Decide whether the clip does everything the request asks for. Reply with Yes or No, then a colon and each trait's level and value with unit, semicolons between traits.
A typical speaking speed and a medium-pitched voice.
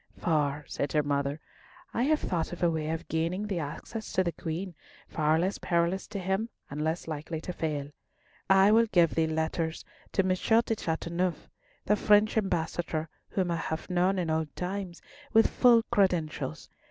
Yes: average, 175 wpm; medium, 170 Hz